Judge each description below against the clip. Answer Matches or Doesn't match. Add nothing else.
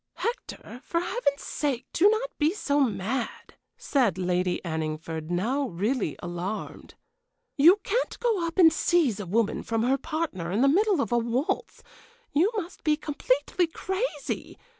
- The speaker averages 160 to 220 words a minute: Doesn't match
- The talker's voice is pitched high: Matches